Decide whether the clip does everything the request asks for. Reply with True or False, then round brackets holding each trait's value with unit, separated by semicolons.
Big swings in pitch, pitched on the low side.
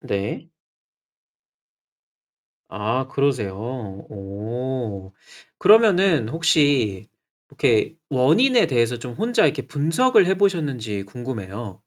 True (7.5 semitones; 130 Hz)